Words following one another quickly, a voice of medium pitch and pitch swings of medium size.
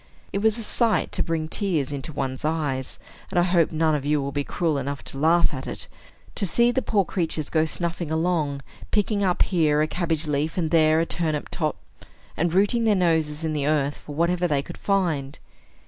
Yes: fast, 210 wpm; medium, 160 Hz; average, 3.2 semitones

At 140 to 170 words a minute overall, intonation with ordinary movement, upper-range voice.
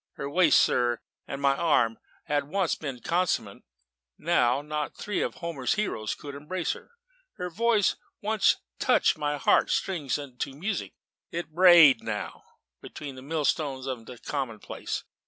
No: average, 155 wpm; average, 4.5 semitones; medium, 150 Hz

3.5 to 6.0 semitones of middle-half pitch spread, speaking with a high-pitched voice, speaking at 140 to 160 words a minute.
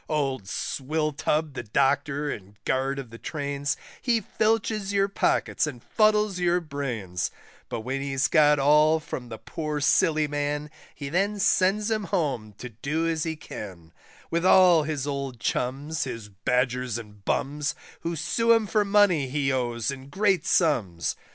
No: average, 4.8 semitones; medium, 145 Hz; average, 155 wpm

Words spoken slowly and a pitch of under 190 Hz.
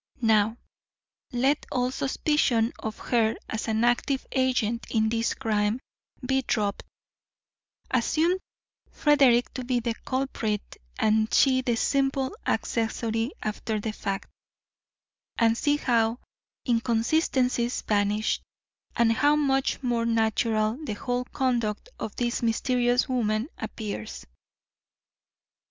No: slow, 110 wpm; high, 235 Hz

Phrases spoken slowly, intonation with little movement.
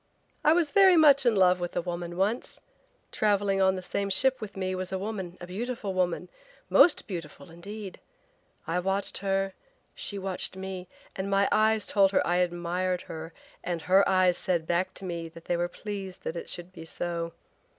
No: average, 185 wpm; narrow, 2.3 semitones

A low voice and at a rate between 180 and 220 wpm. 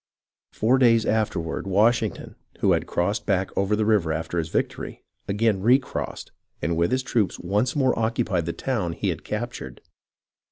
No: low, 105 Hz; average, 160 wpm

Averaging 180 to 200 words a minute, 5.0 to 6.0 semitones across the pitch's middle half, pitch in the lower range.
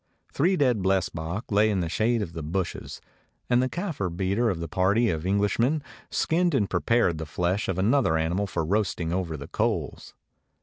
Yes: average, 185 wpm; wide, 5.5 semitones; very low, 95 Hz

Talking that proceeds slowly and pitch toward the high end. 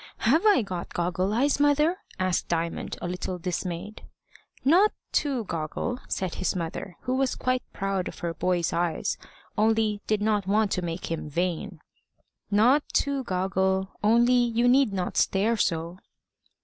No: average, 150 wpm; high, 195 Hz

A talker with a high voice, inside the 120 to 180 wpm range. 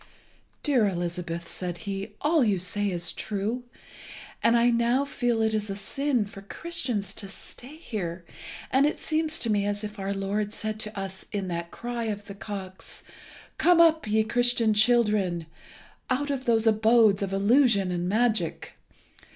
Yes: high, 215 Hz; average, 165 wpm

